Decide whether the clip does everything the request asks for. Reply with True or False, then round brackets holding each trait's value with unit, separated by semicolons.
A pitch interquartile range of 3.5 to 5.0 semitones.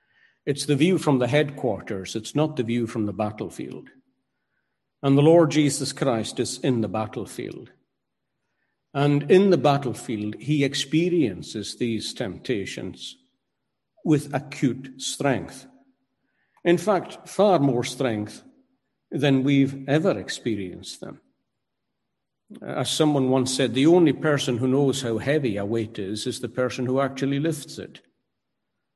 True (4.0 semitones)